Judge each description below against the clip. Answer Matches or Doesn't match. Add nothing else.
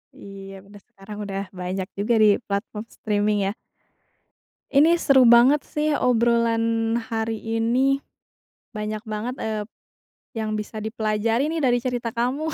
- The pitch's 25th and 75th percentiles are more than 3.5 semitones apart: Doesn't match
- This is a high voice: Matches